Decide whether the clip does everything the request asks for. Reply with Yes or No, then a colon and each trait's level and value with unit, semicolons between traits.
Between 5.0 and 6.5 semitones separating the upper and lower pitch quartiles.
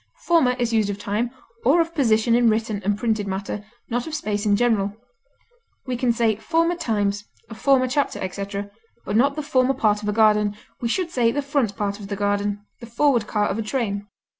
No: average, 3.8 semitones